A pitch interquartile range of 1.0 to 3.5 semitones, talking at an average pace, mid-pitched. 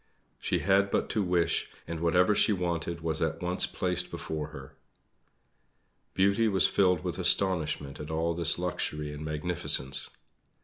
No: average, 2.9 semitones; average, 145 wpm; very low, 85 Hz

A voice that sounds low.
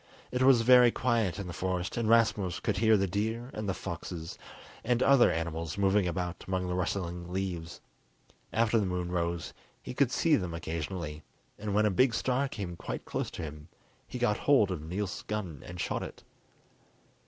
Yes: very low, 95 Hz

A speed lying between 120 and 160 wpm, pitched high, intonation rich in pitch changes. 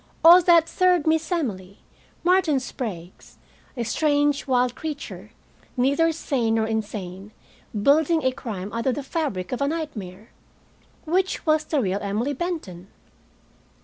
Yes: slow, 135 wpm; very high, 265 Hz; wide, 7.1 semitones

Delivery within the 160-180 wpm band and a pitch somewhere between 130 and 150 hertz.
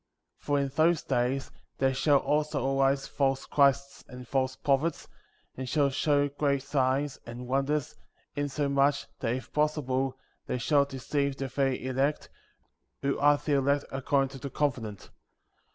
No: average, 150 wpm; medium, 140 Hz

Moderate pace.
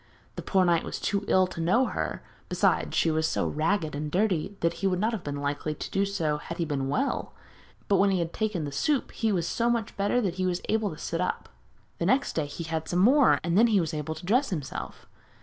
No: fast, 250 wpm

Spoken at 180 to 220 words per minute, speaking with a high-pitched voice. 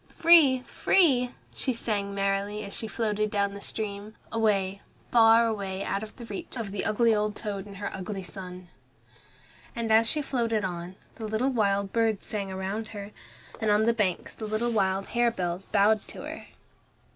No: average, 170 wpm; high, 210 Hz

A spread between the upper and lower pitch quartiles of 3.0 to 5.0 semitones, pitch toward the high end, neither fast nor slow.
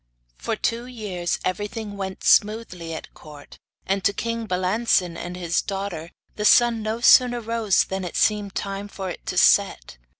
Yes: average, 3.5 semitones; high, 200 Hz; average, 165 wpm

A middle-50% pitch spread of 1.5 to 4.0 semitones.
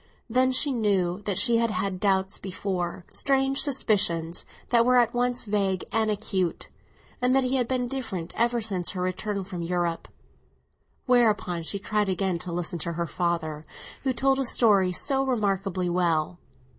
No: wide, 5.4 semitones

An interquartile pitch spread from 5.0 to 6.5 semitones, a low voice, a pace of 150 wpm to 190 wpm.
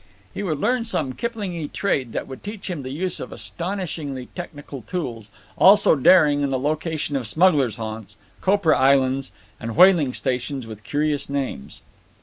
No: wide, 5.6 semitones; medium, 145 Hz; average, 155 wpm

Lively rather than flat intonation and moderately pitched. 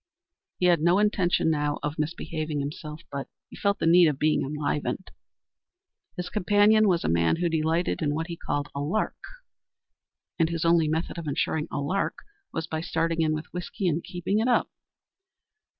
No: average, 2.7 semitones; medium, 165 Hz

